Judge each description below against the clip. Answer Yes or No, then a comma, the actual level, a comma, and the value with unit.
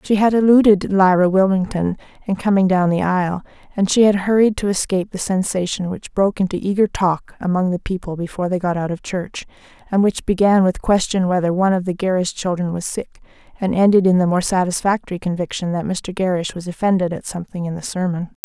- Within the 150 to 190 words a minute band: No, average, 200 wpm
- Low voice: No, medium, 185 Hz